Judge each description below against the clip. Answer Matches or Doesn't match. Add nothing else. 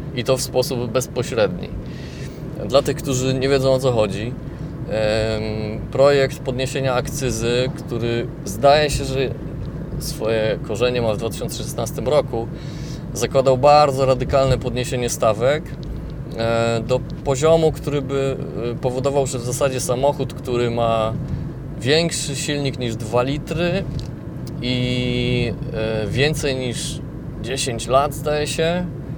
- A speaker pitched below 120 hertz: Doesn't match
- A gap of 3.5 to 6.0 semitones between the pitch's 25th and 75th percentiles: Doesn't match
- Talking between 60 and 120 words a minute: Matches